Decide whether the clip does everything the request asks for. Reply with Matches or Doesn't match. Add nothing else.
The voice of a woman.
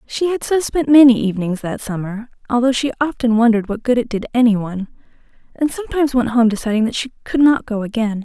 Matches